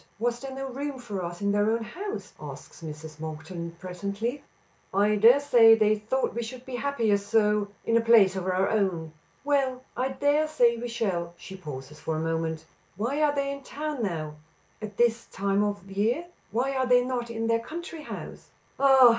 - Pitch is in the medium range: No, high, 225 Hz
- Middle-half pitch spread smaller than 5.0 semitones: No, wide, 5.4 semitones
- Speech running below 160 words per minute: No, average, 190 wpm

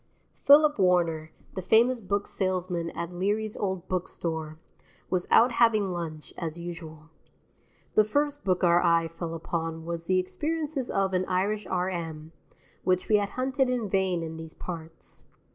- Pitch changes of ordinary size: Yes, average, 4.1 semitones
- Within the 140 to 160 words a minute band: Yes, average, 155 wpm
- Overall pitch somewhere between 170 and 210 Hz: Yes, medium, 185 Hz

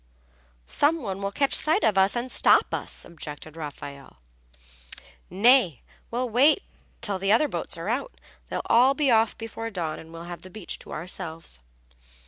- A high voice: Yes, high, 200 Hz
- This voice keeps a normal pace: Yes, average, 165 wpm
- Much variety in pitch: Yes, wide, 6.9 semitones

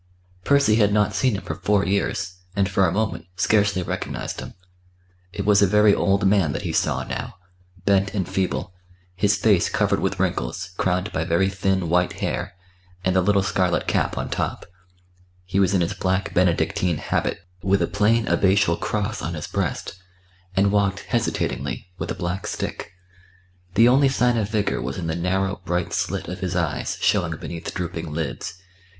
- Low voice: Yes, very low, 95 Hz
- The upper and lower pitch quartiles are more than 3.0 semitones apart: No, narrow, 2.5 semitones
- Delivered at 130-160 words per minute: No, average, 180 wpm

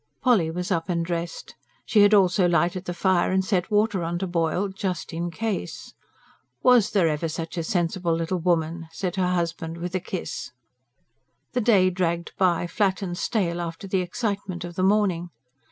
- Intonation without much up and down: Yes, narrow, 2.3 semitones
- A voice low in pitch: No, medium, 180 Hz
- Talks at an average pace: Yes, average, 180 wpm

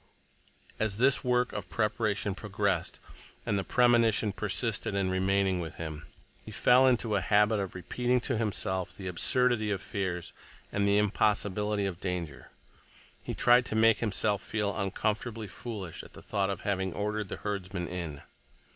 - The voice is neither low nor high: No, low, 105 Hz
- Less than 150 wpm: No, average, 155 wpm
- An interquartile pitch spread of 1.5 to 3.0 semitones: Yes, narrow, 2.6 semitones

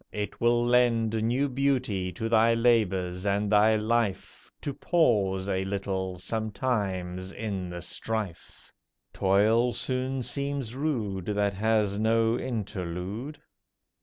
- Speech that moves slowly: Yes, slow, 115 wpm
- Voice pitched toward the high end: No, low, 110 Hz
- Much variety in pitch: No, average, 3.7 semitones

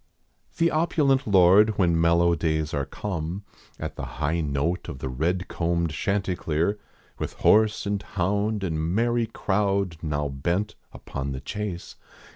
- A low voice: Yes, very low, 90 Hz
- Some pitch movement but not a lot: Yes, average, 4.6 semitones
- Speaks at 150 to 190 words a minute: No, slow, 135 wpm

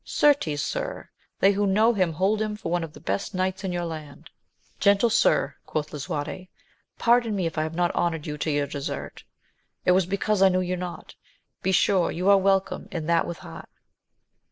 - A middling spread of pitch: Yes, average, 3.6 semitones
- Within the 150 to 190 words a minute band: No, average, 200 wpm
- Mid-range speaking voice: Yes, medium, 180 Hz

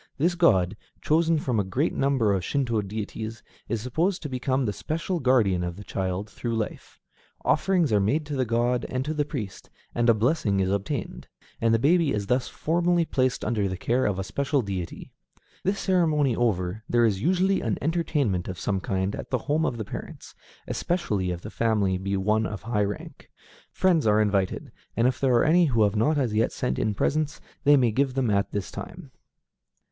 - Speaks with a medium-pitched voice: No, low, 120 Hz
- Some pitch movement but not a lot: No, wide, 6.3 semitones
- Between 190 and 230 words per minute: Yes, average, 200 wpm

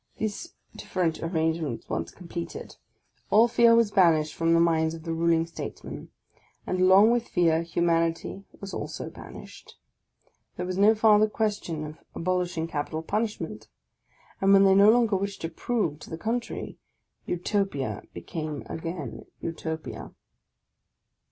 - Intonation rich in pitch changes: No, average, 3.9 semitones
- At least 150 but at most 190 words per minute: No, slow, 135 wpm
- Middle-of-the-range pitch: Yes, medium, 170 Hz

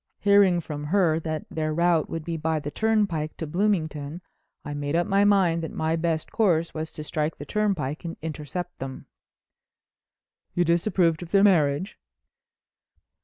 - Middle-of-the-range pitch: Yes, medium, 165 Hz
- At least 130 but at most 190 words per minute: Yes, average, 160 wpm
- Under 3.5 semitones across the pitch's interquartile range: Yes, average, 2.8 semitones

